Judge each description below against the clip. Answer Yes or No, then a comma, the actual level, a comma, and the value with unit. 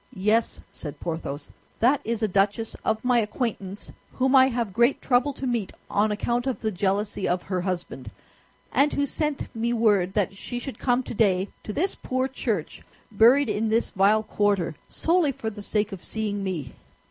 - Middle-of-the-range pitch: No, high, 220 Hz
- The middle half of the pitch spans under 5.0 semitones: Yes, average, 3.9 semitones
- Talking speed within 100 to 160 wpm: No, average, 180 wpm